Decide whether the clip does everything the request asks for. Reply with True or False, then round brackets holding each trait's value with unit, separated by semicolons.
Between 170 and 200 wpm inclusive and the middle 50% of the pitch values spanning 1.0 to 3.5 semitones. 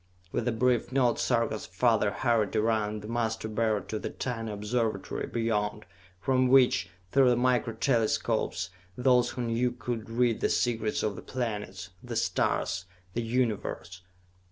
False (150 wpm; 2.4 semitones)